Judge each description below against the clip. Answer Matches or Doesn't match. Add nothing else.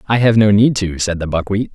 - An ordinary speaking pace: Doesn't match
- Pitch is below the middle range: Matches